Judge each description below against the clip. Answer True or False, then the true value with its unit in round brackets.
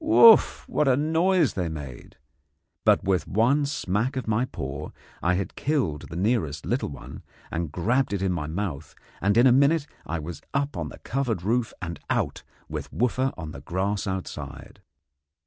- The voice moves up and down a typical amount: False (7.9 semitones)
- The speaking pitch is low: True (100 Hz)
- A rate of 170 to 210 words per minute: True (175 wpm)